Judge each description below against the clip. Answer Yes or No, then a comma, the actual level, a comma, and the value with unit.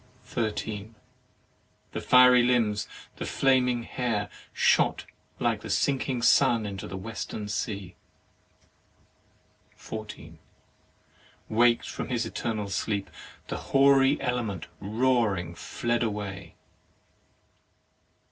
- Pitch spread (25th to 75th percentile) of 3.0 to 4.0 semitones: Yes, average, 3.3 semitones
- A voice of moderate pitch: No, low, 115 Hz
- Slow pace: Yes, slow, 90 wpm